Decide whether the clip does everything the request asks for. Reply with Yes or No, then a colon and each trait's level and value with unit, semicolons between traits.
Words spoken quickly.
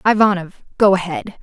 No: slow, 125 wpm